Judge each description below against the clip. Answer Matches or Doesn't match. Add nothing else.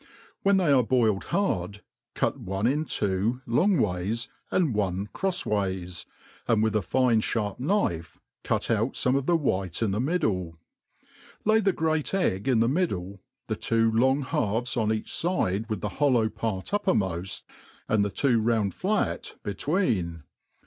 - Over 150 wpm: Matches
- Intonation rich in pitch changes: Matches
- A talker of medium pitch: Doesn't match